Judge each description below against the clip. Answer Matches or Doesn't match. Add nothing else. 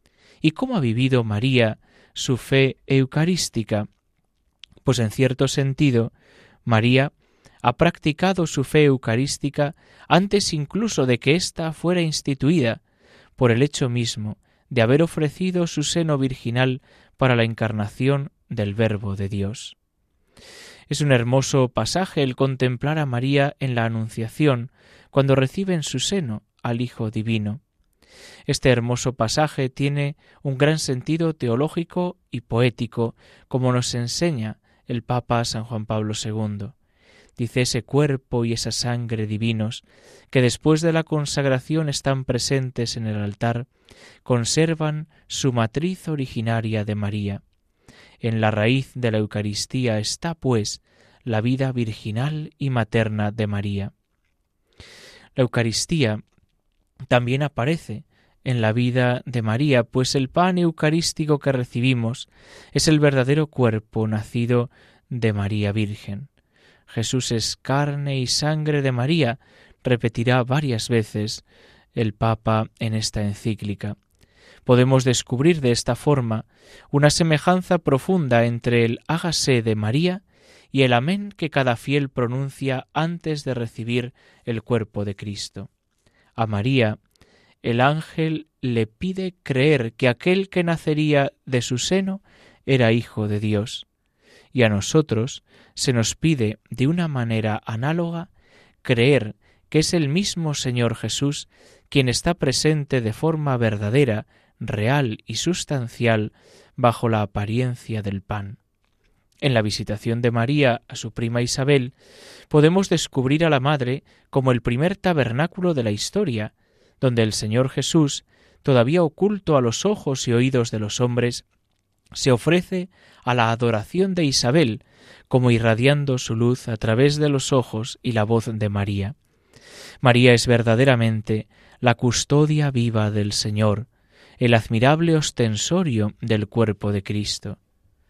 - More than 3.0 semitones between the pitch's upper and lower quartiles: Matches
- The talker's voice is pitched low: Matches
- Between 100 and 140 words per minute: Matches